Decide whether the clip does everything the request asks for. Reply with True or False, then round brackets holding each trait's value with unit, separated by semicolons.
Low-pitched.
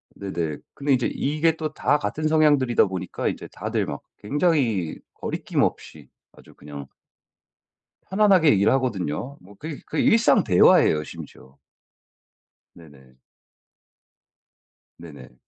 True (120 Hz)